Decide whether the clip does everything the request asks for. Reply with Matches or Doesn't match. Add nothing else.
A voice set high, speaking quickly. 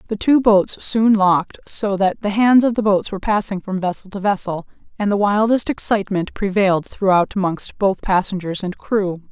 Doesn't match